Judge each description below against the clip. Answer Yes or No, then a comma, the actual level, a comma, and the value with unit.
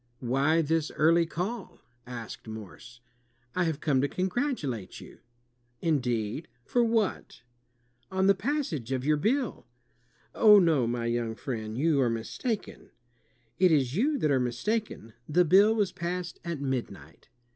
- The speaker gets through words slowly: No, average, 145 wpm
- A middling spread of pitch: No, wide, 7.6 semitones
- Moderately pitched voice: Yes, medium, 155 Hz